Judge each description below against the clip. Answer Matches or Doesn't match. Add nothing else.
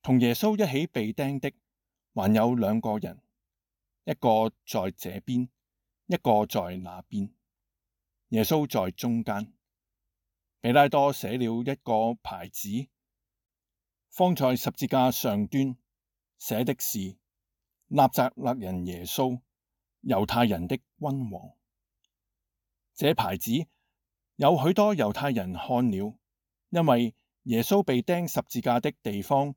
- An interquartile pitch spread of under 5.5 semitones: Matches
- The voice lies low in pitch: Matches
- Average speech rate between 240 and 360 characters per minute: Doesn't match